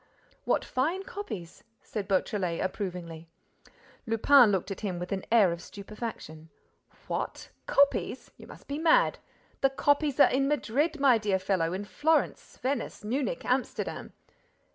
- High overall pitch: Yes, high, 220 Hz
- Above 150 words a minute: No, average, 140 wpm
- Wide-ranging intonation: Yes, wide, 7.1 semitones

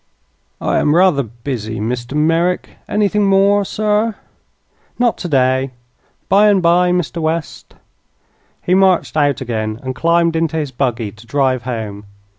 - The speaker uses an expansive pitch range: Yes, wide, 6.5 semitones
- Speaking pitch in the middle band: Yes, medium, 155 Hz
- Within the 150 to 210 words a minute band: No, slow, 135 wpm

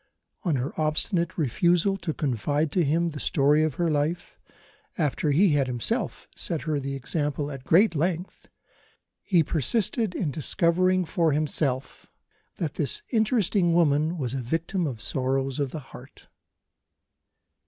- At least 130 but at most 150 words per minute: Yes, average, 145 wpm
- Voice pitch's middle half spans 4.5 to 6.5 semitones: No, average, 3.7 semitones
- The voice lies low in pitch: No, medium, 155 Hz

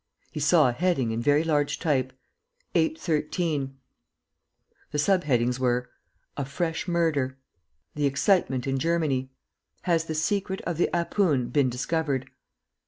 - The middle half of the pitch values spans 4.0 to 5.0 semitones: Yes, average, 4.3 semitones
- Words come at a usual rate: No, slow, 130 wpm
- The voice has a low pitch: No, medium, 150 Hz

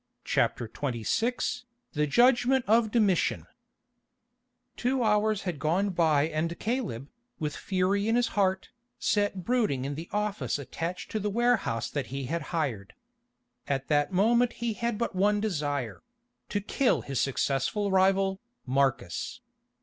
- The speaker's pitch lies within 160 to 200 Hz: Yes, high, 190 Hz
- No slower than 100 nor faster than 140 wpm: Yes, slow, 135 wpm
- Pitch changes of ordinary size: No, wide, 7.3 semitones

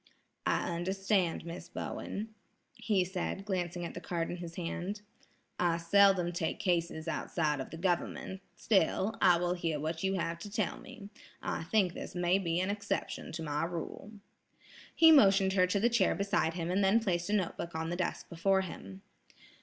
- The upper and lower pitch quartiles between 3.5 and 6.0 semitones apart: No, average, 2.8 semitones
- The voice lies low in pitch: No, medium, 180 Hz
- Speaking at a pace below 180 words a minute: No, average, 185 wpm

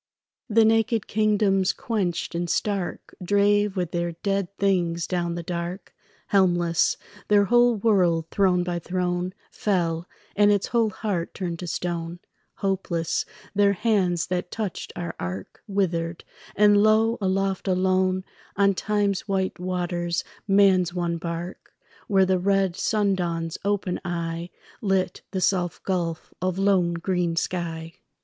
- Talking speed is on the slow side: Yes, slow, 130 wpm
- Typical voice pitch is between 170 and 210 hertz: Yes, medium, 185 Hz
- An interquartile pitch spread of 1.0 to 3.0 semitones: Yes, narrow, 2.5 semitones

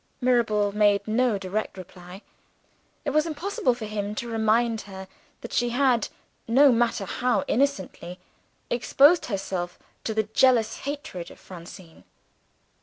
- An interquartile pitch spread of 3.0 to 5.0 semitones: Yes, average, 4.1 semitones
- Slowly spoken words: Yes, slow, 130 wpm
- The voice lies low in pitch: No, high, 220 Hz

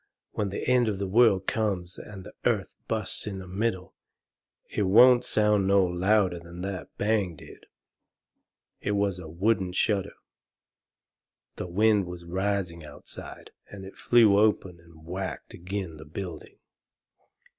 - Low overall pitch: Yes, very low, 95 Hz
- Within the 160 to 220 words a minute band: No, average, 145 wpm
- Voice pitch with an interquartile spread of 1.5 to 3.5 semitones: Yes, average, 3.0 semitones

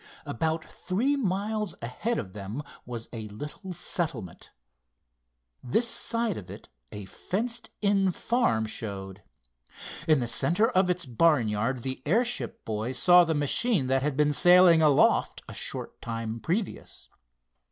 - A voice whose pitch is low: No, medium, 155 Hz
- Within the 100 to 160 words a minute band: Yes, slow, 135 wpm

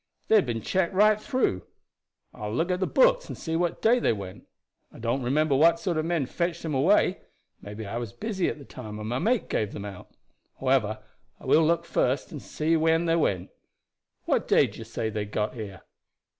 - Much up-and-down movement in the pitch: Yes, wide, 7.9 semitones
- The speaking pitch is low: No, medium, 155 Hz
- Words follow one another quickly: Yes, fast, 215 wpm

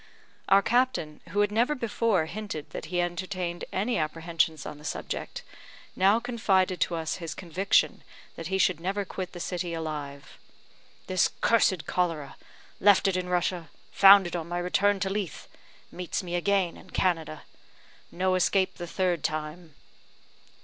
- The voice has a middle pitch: Yes, medium, 180 Hz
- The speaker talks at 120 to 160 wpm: Yes, average, 155 wpm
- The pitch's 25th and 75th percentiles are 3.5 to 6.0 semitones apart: No, average, 2.9 semitones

